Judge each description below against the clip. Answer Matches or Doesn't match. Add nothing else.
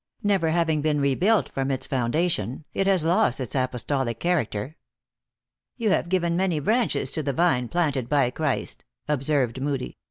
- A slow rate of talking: Doesn't match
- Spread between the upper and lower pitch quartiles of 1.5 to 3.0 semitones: Doesn't match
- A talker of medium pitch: Matches